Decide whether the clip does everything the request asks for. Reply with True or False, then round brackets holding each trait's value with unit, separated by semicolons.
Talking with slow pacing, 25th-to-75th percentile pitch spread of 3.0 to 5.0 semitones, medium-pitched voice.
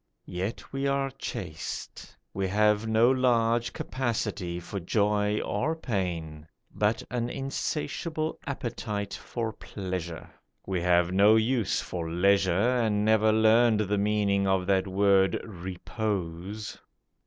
False (120 wpm; 3.7 semitones; 105 Hz)